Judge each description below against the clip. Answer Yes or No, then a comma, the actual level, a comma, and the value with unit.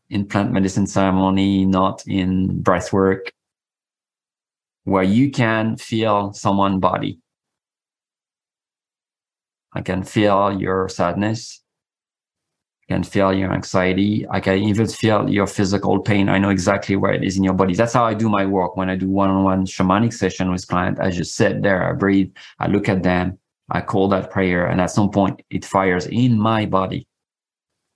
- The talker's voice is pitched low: Yes, very low, 95 Hz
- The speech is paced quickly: No, average, 170 wpm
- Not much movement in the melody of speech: Yes, narrow, 1.3 semitones